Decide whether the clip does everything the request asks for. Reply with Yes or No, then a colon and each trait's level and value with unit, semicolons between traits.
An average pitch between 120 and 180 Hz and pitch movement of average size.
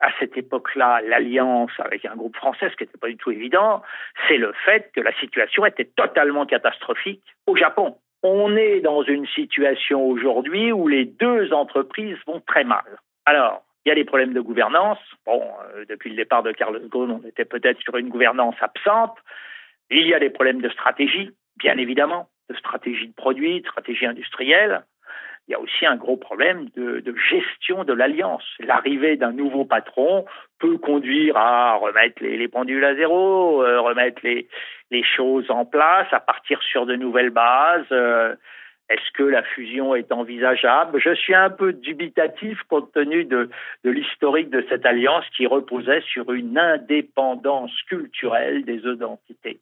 No: low, 135 Hz; wide, 6.9 semitones